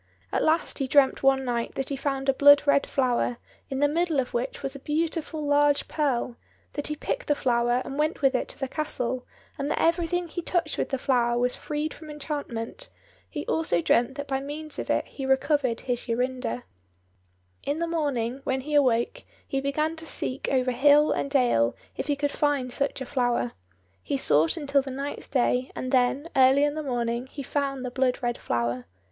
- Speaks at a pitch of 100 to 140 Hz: No, very high, 275 Hz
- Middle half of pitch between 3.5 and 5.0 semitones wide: No, average, 2.9 semitones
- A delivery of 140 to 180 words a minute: No, average, 200 wpm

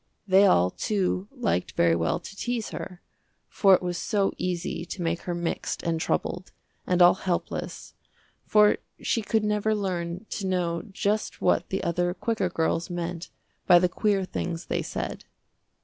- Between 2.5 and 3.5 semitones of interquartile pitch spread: Yes, average, 2.9 semitones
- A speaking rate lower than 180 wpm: Yes, average, 165 wpm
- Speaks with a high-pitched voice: No, medium, 180 Hz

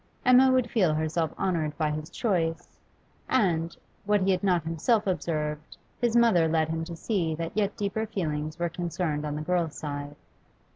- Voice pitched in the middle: Yes, medium, 170 Hz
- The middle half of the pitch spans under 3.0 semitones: No, average, 4.2 semitones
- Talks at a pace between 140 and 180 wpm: Yes, average, 175 wpm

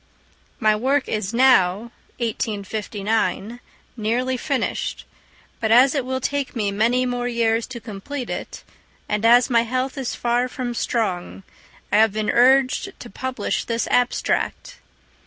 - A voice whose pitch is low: No, high, 235 Hz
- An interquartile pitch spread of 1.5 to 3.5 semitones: Yes, average, 2.8 semitones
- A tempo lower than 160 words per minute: Yes, average, 140 wpm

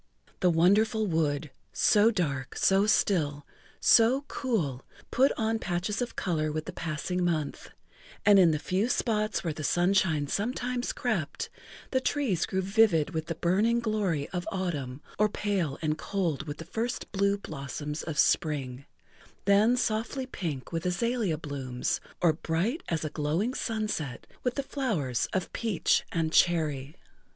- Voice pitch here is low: No, medium, 180 Hz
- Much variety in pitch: Yes, wide, 5.9 semitones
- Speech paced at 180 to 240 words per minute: No, average, 150 wpm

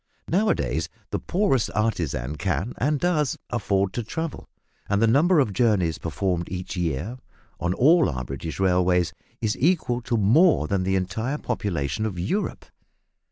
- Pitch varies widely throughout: Yes, wide, 6.5 semitones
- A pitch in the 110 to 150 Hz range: No, low, 100 Hz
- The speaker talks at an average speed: Yes, average, 160 wpm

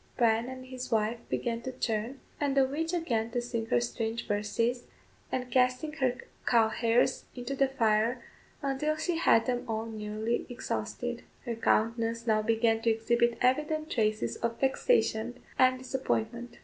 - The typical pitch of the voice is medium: No, high, 240 Hz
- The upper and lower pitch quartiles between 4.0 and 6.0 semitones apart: No, narrow, 2.5 semitones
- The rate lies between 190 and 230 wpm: No, average, 155 wpm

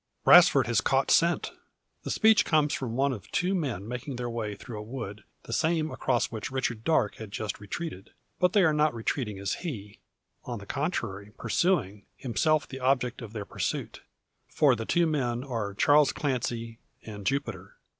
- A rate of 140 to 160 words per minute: No, average, 175 wpm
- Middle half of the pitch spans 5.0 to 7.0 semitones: Yes, wide, 5.6 semitones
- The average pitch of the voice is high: No, low, 120 Hz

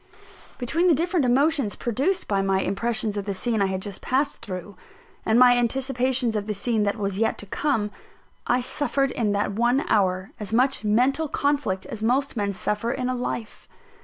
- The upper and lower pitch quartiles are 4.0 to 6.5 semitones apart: Yes, average, 4.4 semitones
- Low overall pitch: No, high, 235 Hz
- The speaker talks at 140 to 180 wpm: No, average, 190 wpm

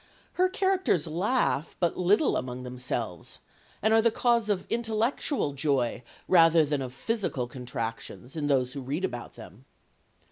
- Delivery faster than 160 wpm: No, average, 145 wpm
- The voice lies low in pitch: No, medium, 155 Hz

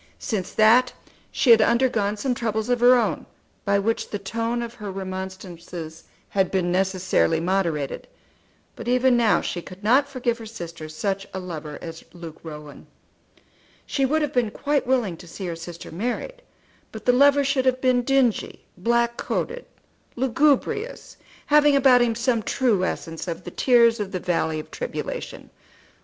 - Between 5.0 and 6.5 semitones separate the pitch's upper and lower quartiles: Yes, wide, 5.5 semitones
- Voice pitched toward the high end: Yes, high, 220 Hz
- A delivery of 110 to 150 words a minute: No, average, 165 wpm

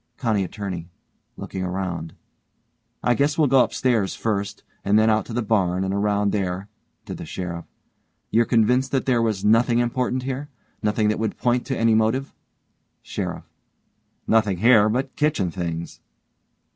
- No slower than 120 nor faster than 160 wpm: Yes, average, 155 wpm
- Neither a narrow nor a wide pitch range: Yes, average, 4.0 semitones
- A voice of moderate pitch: No, low, 110 Hz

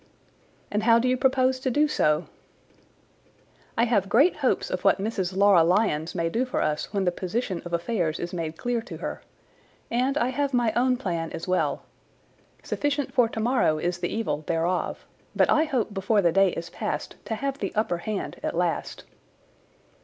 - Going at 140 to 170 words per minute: No, average, 185 wpm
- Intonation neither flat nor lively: No, wide, 6.2 semitones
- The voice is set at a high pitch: Yes, high, 210 Hz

